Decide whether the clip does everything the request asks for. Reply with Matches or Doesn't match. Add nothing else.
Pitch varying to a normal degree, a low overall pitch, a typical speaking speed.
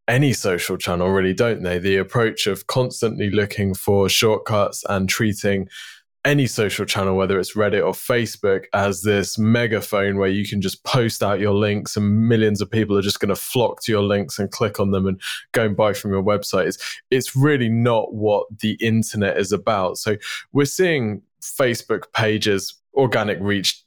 Doesn't match